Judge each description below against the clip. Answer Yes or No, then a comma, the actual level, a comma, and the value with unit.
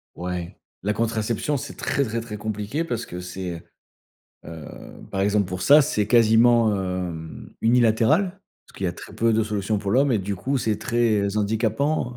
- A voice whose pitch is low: Yes, low, 110 Hz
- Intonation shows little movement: No, average, 3.4 semitones